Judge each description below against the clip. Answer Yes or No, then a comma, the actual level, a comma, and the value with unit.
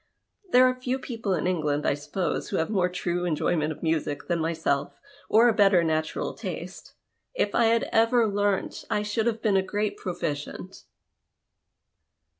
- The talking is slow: No, average, 165 wpm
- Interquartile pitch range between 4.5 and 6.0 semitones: Yes, wide, 5.6 semitones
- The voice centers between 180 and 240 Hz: Yes, high, 190 Hz